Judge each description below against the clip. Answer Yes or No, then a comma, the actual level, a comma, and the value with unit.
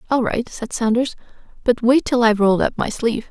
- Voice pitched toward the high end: Yes, high, 235 Hz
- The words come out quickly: Yes, fast, 220 wpm